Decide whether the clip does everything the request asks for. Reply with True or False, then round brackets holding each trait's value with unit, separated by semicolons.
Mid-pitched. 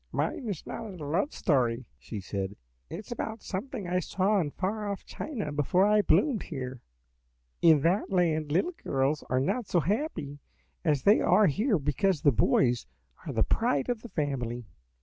True (170 Hz)